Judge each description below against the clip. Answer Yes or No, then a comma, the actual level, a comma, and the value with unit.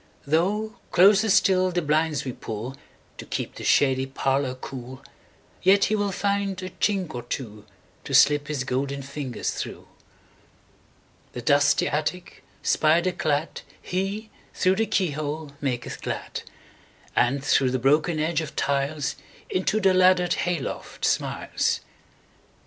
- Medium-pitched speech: Yes, medium, 155 Hz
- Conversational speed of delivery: No, slow, 115 wpm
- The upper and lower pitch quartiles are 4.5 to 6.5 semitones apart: Yes, average, 5.2 semitones